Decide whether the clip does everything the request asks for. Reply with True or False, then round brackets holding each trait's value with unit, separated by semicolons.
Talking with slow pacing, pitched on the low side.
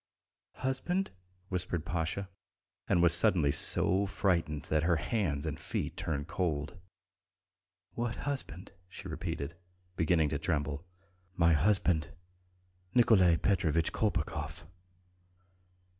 True (100 wpm; 85 Hz)